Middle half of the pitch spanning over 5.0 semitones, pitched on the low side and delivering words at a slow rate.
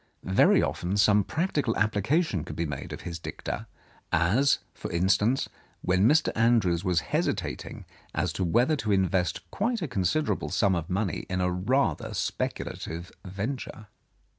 No: wide, 5.6 semitones; low, 100 Hz; average, 150 wpm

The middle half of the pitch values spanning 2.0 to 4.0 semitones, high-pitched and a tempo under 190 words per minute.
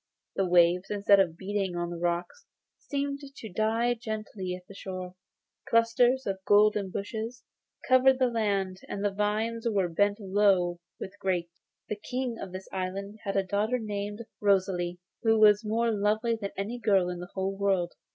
Yes: average, 2.9 semitones; high, 205 Hz; average, 170 wpm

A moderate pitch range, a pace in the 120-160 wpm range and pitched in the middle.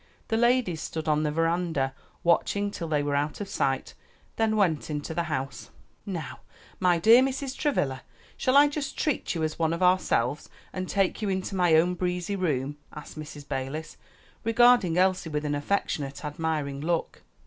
No: average, 5.0 semitones; average, 170 wpm; medium, 170 Hz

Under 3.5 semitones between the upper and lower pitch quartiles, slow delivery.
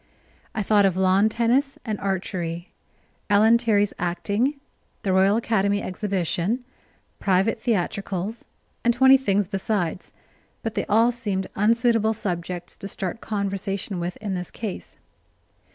Yes: average, 3.1 semitones; slow, 125 wpm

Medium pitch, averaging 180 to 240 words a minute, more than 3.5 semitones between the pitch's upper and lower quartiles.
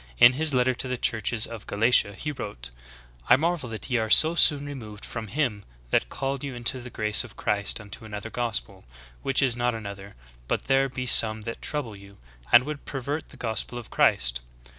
No: low, 120 Hz; average, 200 wpm; average, 4.0 semitones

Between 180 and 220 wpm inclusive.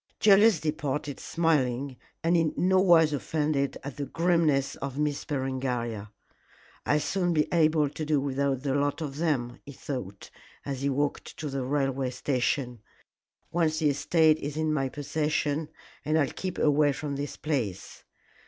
No: average, 155 wpm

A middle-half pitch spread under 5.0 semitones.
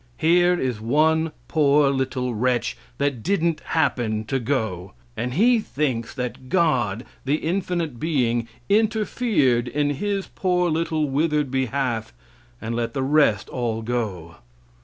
No: average, 5.3 semitones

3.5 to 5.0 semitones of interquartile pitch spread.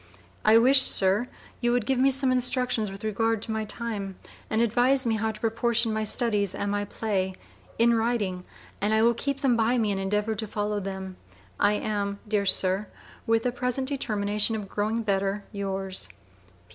No: average, 2.7 semitones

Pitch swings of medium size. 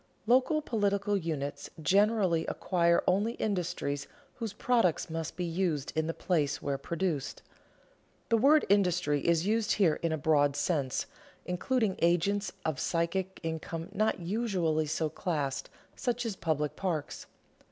Yes: average, 4.4 semitones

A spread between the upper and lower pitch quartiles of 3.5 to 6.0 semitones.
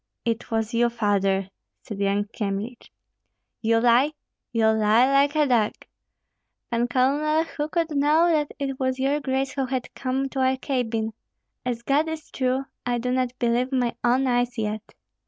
No: average, 3.0 semitones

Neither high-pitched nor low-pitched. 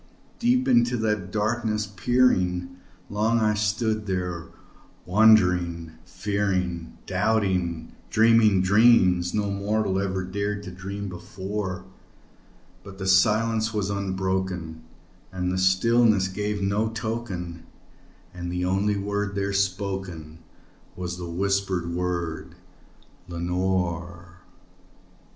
No: very low, 95 Hz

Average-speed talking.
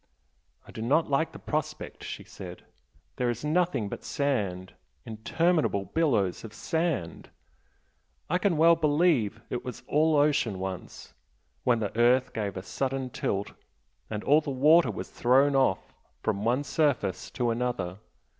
Yes: average, 145 wpm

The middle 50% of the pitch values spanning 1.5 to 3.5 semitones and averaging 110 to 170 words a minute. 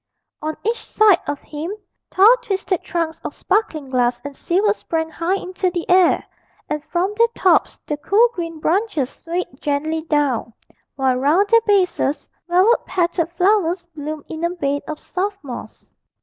No: average, 4.4 semitones; average, 160 wpm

